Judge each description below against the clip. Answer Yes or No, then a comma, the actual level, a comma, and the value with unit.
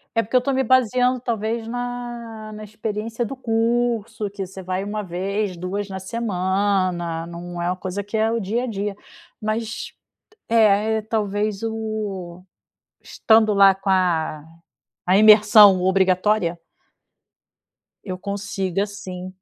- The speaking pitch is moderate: No, high, 205 Hz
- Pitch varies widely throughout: No, average, 3.0 semitones